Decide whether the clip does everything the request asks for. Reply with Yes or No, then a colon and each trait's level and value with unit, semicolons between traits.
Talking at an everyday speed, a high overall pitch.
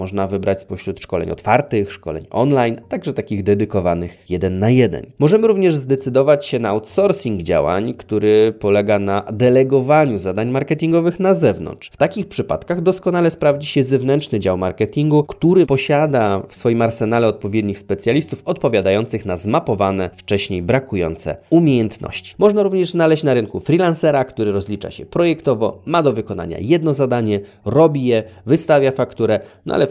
No: average, 145 wpm; low, 120 Hz